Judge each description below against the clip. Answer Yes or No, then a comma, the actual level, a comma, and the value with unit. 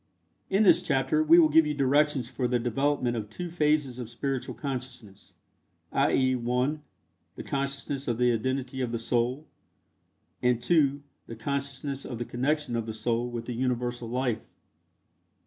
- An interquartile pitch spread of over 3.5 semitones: No, average, 2.8 semitones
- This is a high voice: No, low, 130 Hz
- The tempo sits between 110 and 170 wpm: Yes, average, 160 wpm